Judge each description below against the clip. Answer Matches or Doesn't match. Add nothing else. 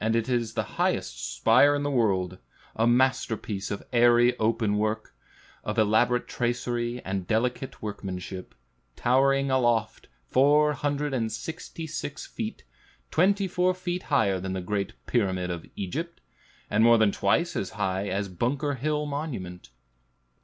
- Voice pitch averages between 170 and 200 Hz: Doesn't match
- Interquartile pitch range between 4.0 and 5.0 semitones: Doesn't match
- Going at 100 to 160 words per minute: Matches